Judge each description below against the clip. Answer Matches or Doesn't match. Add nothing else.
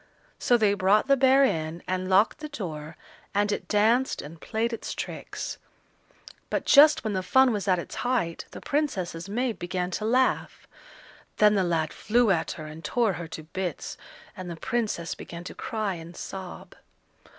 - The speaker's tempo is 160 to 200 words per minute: Matches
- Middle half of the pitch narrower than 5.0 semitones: Doesn't match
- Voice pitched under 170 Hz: Doesn't match